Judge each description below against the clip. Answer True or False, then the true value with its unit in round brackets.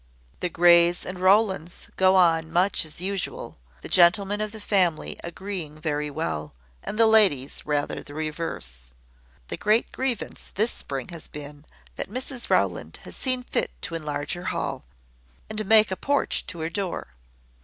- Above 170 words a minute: False (160 wpm)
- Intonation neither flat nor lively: True (4.9 semitones)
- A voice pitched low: False (175 Hz)